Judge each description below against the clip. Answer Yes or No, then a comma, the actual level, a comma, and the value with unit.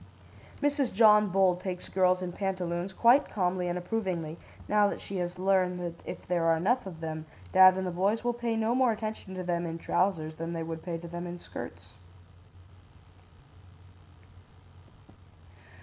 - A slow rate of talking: No, average, 165 wpm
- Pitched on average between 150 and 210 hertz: Yes, medium, 185 Hz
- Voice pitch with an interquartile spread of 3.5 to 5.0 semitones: No, average, 3.1 semitones